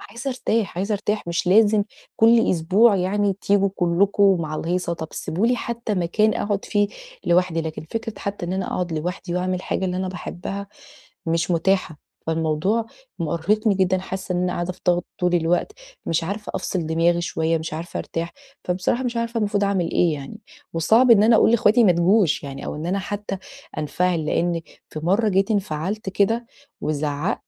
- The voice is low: No, medium, 185 Hz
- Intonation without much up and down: No, average, 3.5 semitones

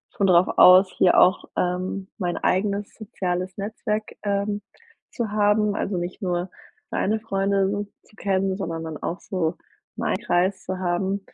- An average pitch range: No, narrow, 2.1 semitones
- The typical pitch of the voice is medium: No, high, 195 Hz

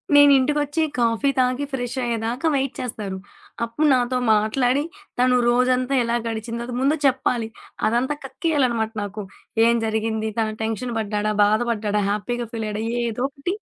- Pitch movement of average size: Yes, average, 3.0 semitones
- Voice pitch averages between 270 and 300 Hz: No, high, 240 Hz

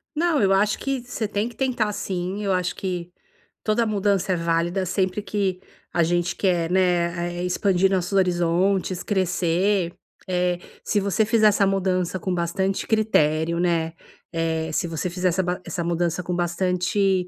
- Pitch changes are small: Yes, narrow, 2.3 semitones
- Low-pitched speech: No, medium, 185 Hz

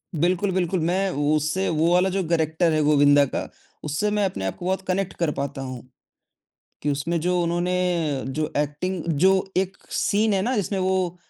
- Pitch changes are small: No, average, 3.8 semitones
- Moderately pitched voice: Yes, medium, 175 Hz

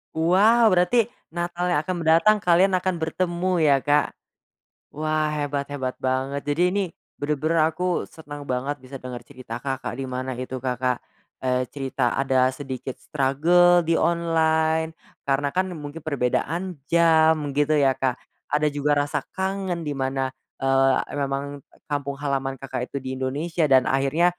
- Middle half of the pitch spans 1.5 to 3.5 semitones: No, average, 3.9 semitones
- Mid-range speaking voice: Yes, medium, 145 Hz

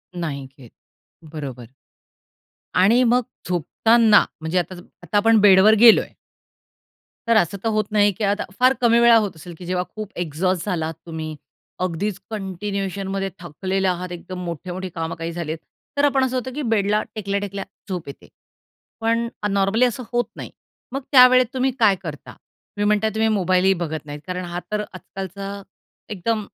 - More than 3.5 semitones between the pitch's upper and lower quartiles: Yes, average, 3.9 semitones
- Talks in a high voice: Yes, high, 195 Hz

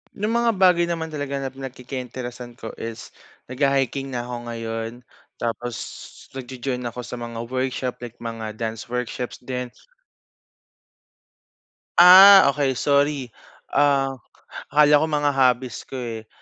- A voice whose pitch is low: Yes, low, 130 Hz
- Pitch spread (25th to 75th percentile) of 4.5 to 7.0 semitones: No, average, 3.0 semitones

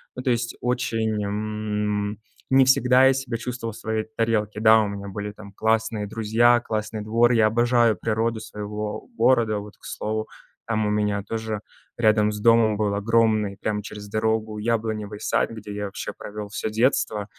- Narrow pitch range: Yes, narrow, 1.6 semitones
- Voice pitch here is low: Yes, low, 110 Hz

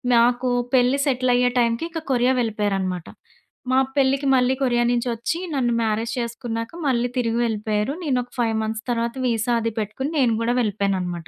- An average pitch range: No, narrow, 2.3 semitones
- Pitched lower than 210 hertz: No, high, 235 Hz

